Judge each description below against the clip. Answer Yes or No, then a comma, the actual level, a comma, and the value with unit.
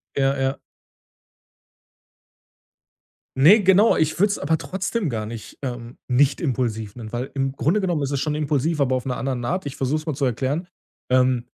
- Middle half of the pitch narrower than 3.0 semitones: No, average, 3.8 semitones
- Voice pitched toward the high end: No, low, 135 Hz